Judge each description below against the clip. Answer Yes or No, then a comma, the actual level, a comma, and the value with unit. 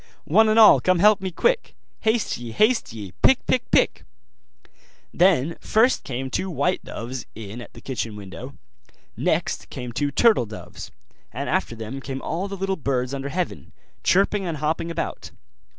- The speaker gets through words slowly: No, average, 165 wpm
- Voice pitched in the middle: Yes, medium, 155 Hz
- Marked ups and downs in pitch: Yes, wide, 7.8 semitones